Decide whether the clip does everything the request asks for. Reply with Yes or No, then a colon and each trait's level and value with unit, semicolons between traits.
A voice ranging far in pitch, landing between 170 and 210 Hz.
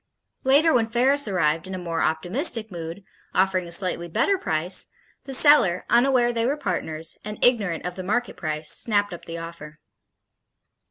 Yes: wide, 6.3 semitones; high, 190 Hz